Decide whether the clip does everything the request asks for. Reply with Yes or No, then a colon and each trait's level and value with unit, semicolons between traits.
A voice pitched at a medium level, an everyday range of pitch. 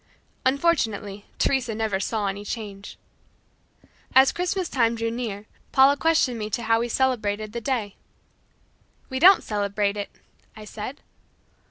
No: high, 225 Hz; average, 4.2 semitones